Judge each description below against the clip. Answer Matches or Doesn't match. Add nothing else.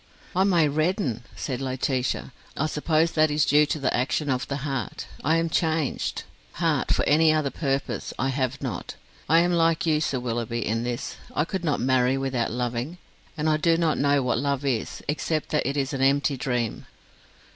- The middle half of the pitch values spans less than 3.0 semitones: Doesn't match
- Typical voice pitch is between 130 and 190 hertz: Matches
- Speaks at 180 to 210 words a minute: Matches